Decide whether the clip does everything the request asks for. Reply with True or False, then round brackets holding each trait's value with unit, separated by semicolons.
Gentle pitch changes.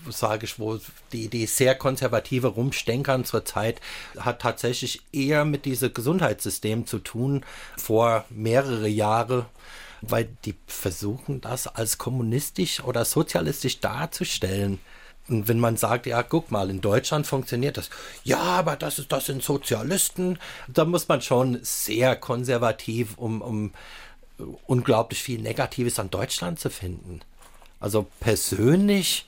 False (3.4 semitones)